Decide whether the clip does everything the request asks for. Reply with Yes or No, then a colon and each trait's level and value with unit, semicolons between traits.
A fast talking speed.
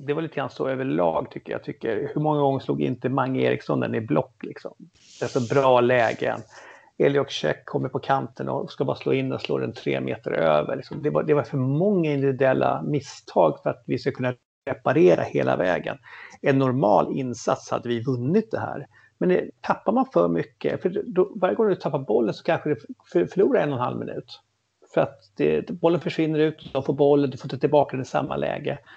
Yes: fast, 220 wpm